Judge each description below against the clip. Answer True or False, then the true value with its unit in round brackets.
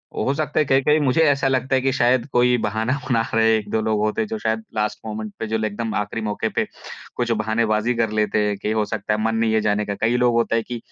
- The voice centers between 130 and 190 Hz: False (115 Hz)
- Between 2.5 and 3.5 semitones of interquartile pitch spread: True (2.8 semitones)